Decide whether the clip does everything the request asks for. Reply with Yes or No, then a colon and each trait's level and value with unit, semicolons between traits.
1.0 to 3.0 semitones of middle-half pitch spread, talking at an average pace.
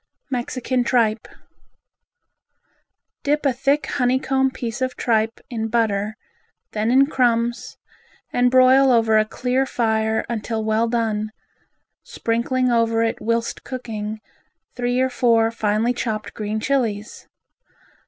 No: narrow, 2.5 semitones; slow, 120 wpm